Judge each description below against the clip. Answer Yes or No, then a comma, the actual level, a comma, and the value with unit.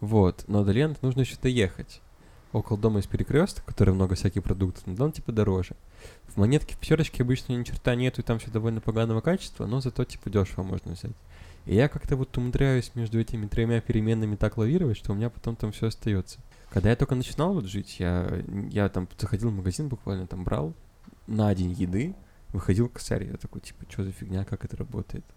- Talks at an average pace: No, fast, 205 wpm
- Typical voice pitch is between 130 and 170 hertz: No, low, 110 Hz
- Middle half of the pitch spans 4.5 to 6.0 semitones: No, average, 4.0 semitones